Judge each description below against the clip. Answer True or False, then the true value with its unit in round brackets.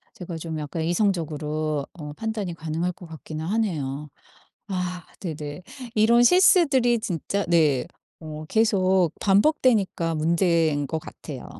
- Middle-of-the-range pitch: True (170 Hz)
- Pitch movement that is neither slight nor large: True (4.6 semitones)